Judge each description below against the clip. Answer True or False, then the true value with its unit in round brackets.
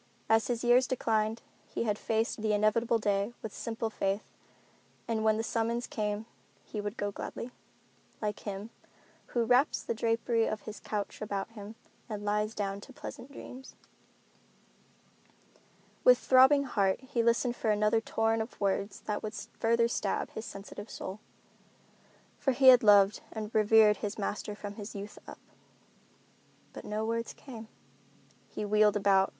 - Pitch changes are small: True (2.0 semitones)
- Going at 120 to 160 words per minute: True (155 wpm)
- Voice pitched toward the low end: False (220 Hz)